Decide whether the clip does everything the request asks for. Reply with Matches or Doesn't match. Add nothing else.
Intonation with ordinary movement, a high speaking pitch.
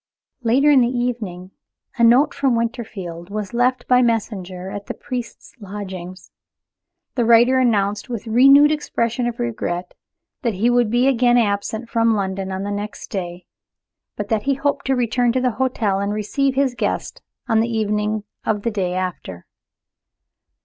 Matches